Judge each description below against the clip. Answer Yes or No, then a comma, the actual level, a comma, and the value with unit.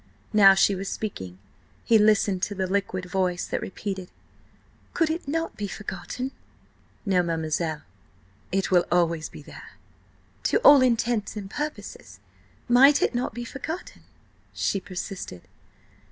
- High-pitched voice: Yes, high, 195 Hz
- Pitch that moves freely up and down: No, average, 5.0 semitones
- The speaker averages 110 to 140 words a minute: Yes, slow, 135 wpm